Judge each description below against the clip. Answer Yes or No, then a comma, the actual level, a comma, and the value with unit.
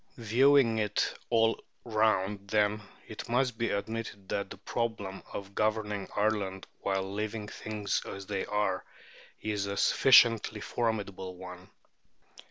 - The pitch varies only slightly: Yes, narrow, 2.1 semitones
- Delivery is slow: Yes, slow, 125 wpm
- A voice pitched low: Yes, low, 105 Hz